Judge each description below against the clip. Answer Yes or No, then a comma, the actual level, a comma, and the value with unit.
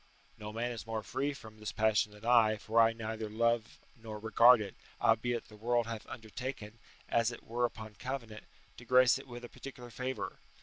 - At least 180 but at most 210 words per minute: Yes, average, 190 wpm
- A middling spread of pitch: No, narrow, 1.9 semitones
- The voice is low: Yes, low, 115 Hz